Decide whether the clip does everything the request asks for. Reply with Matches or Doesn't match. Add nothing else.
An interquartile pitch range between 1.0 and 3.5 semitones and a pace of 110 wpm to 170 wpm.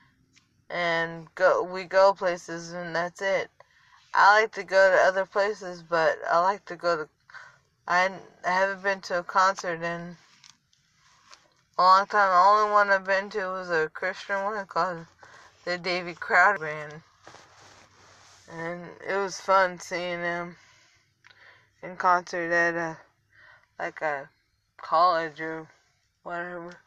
Matches